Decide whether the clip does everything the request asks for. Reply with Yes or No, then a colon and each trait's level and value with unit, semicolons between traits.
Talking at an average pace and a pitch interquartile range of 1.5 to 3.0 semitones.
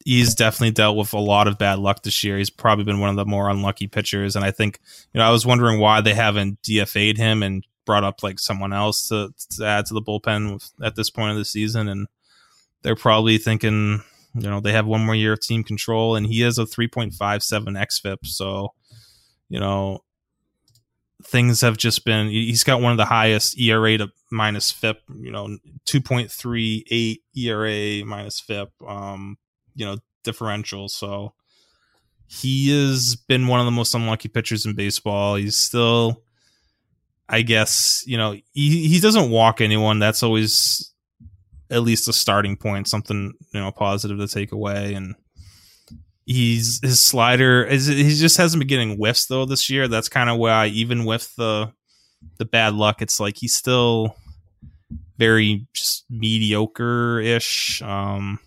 Yes: average, 170 wpm; narrow, 2.4 semitones